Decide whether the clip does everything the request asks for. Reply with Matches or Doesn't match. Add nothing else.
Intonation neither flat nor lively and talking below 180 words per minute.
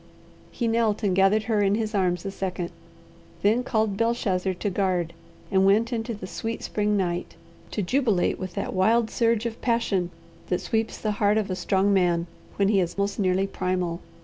Doesn't match